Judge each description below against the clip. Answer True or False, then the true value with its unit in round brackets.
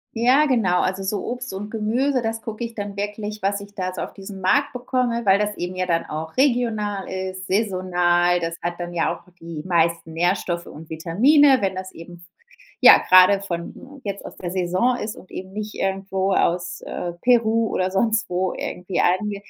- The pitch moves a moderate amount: True (3.8 semitones)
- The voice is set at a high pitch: True (195 Hz)